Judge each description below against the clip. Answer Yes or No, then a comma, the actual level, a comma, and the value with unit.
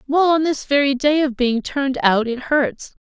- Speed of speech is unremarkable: No, fast, 220 wpm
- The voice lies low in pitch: No, very high, 275 Hz